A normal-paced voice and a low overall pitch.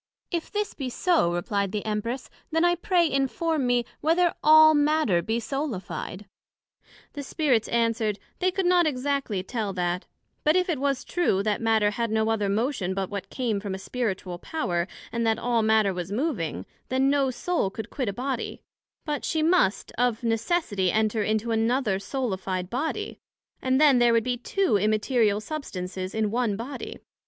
No: average, 170 wpm; high, 235 Hz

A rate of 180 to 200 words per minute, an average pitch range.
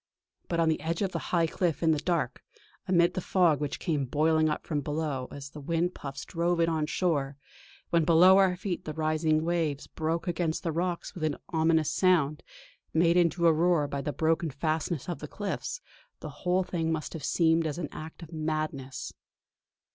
No: average, 195 wpm; narrow, 2.1 semitones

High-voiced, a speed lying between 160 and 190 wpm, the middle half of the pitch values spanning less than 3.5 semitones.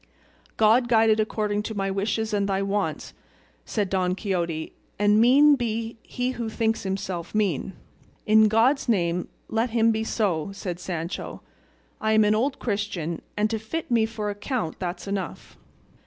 Yes: high, 210 Hz; average, 165 wpm; narrow, 2.6 semitones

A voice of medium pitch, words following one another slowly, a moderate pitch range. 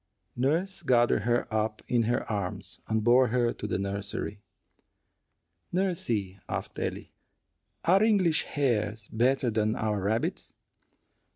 No: low, 115 Hz; slow, 120 wpm; average, 4.2 semitones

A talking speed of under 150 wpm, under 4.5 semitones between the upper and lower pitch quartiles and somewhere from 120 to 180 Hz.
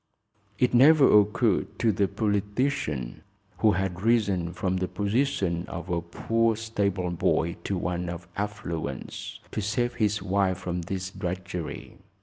No: slow, 135 wpm; average, 3.5 semitones; very low, 95 Hz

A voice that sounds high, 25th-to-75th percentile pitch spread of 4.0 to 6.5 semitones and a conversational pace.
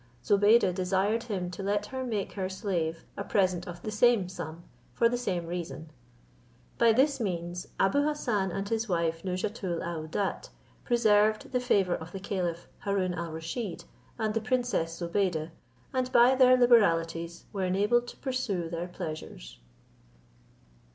Yes: high, 195 Hz; average, 5.0 semitones; average, 150 wpm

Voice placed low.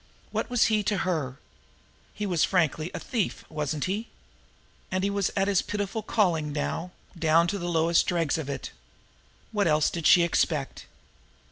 No: medium, 175 Hz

